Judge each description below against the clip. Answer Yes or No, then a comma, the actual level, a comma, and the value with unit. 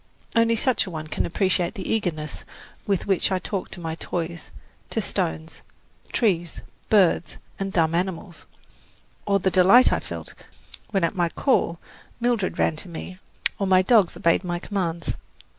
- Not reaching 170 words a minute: Yes, average, 160 wpm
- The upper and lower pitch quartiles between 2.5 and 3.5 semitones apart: Yes, average, 3.0 semitones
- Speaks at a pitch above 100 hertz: Yes, medium, 185 Hz